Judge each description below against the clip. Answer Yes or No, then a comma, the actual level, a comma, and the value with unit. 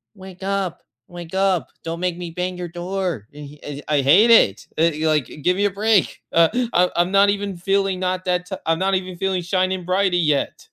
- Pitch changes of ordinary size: No, narrow, 2.3 semitones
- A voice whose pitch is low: No, medium, 180 Hz